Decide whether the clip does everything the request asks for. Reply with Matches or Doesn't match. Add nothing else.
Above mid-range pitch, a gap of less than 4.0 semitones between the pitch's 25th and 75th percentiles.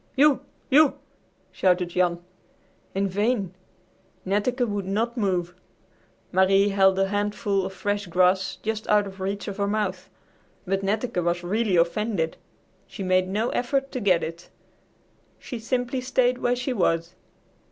Matches